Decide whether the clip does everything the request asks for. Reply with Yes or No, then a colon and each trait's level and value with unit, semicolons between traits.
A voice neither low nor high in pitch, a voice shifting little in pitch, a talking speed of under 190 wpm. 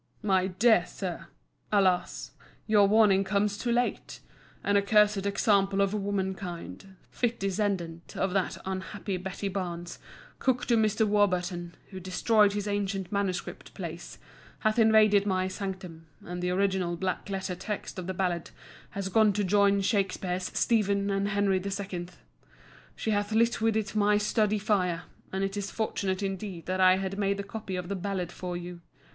No: high, 195 Hz; narrow, 1.9 semitones; average, 155 wpm